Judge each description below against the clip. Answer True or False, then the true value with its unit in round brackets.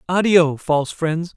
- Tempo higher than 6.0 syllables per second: False (4.2 syllables/s)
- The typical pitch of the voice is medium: True (165 Hz)